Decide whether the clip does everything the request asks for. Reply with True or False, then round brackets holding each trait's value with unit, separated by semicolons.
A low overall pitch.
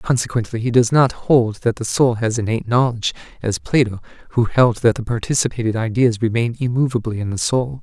True (120 Hz)